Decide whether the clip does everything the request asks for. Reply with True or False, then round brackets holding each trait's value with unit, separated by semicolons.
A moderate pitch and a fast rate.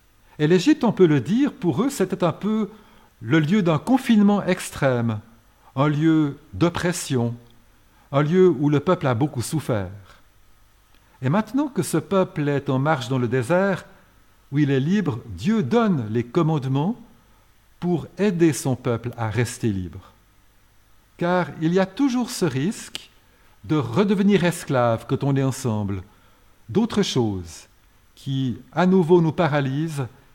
False (145 Hz; 145 wpm)